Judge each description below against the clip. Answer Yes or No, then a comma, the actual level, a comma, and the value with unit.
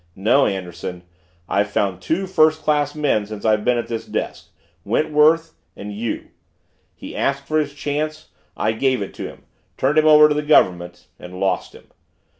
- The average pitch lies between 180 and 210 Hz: No, low, 130 Hz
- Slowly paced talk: No, average, 175 wpm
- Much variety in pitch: Yes, wide, 7.0 semitones